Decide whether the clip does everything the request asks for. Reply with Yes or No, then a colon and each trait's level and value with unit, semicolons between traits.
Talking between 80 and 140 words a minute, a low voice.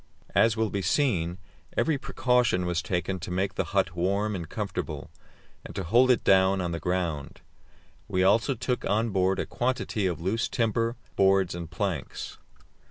No: average, 165 wpm; very low, 95 Hz